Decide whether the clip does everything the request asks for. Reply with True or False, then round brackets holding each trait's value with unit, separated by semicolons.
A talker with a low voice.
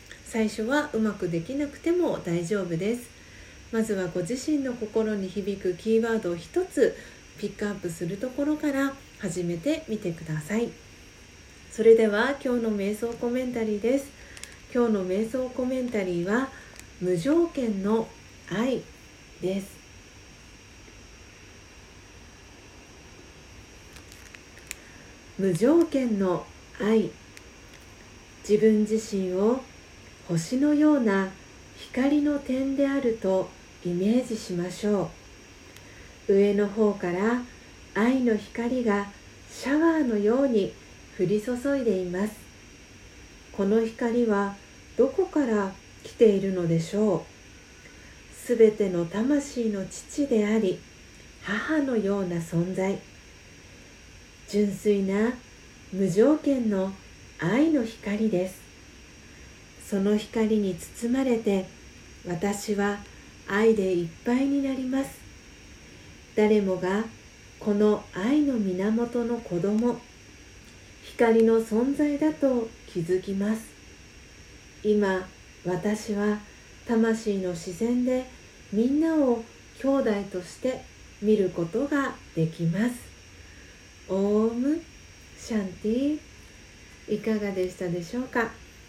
False (210 Hz)